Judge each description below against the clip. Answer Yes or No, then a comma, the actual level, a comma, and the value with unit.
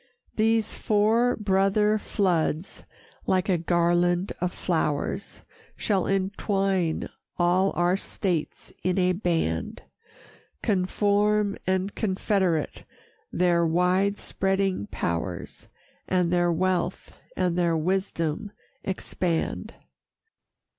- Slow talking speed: Yes, slow, 90 wpm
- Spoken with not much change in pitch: Yes, narrow, 2.3 semitones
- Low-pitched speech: No, medium, 185 Hz